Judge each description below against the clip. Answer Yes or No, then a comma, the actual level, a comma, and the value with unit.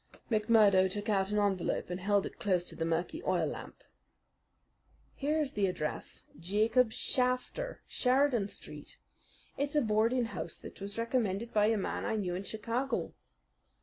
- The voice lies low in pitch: No, high, 215 Hz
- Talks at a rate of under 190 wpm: Yes, average, 155 wpm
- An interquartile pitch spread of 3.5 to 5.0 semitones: Yes, average, 4.4 semitones